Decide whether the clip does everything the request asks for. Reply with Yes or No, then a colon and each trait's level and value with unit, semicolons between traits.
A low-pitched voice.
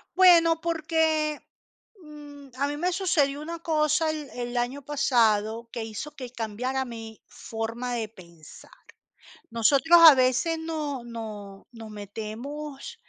No: very high, 270 Hz